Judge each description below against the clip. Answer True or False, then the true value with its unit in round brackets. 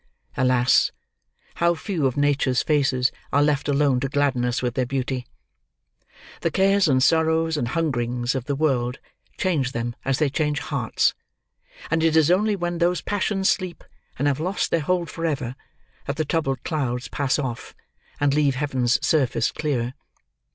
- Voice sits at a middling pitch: True (145 Hz)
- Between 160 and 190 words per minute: True (165 wpm)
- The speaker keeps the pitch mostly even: False (4.0 semitones)